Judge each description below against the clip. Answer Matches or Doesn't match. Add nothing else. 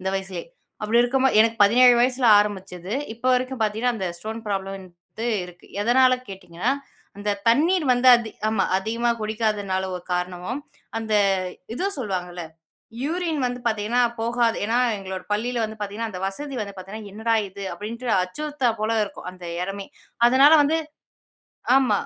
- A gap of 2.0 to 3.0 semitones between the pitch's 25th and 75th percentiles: Doesn't match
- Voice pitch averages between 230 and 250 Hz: Doesn't match